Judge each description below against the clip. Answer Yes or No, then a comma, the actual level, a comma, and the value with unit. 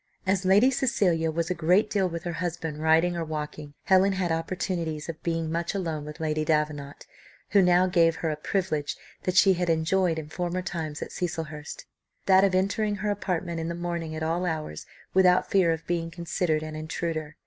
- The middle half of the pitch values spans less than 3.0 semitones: Yes, narrow, 2.6 semitones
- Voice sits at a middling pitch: Yes, medium, 170 Hz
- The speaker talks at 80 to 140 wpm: No, average, 190 wpm